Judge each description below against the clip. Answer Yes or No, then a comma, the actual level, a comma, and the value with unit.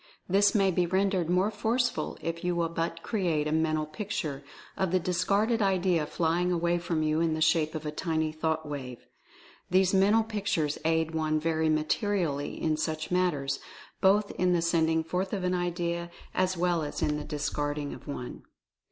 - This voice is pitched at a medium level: Yes, medium, 170 Hz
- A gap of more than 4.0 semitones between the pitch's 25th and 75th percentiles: No, average, 2.9 semitones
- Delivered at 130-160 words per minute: No, average, 180 wpm